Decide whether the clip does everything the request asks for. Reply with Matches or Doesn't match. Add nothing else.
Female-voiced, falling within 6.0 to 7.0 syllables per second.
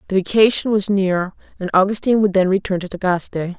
Matches